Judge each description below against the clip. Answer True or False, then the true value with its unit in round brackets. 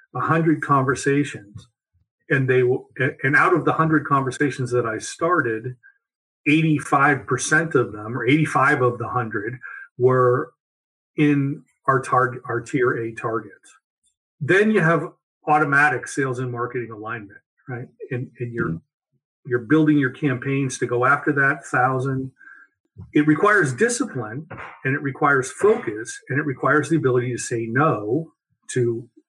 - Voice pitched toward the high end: False (140 Hz)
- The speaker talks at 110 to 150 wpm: True (140 wpm)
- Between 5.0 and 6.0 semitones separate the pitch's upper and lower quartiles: False (3.7 semitones)